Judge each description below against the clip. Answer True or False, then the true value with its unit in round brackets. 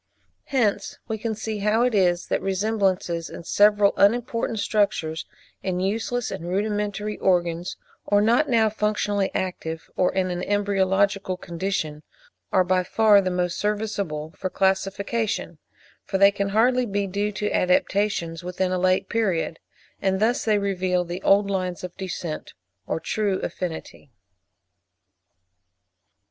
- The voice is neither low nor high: False (195 Hz)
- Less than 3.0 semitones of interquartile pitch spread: True (2.5 semitones)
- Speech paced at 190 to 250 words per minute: False (140 wpm)